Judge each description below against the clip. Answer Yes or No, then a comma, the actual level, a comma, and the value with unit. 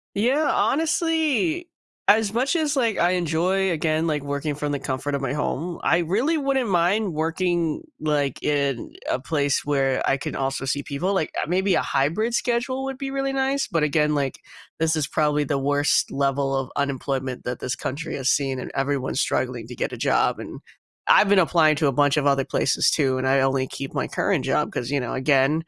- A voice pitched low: No, medium, 150 Hz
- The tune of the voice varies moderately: No, wide, 6.3 semitones